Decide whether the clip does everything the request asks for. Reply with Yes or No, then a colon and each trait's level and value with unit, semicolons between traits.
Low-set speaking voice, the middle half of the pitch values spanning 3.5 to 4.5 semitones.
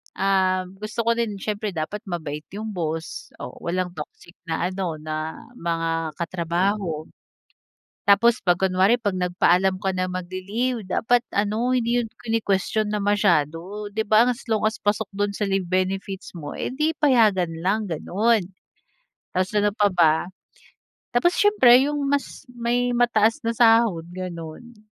No: high, 200 Hz; average, 4.2 semitones